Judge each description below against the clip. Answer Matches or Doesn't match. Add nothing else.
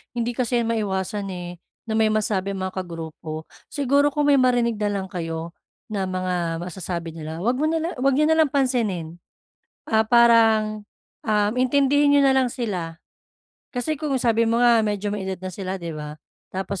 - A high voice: Matches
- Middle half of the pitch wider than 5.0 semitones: Matches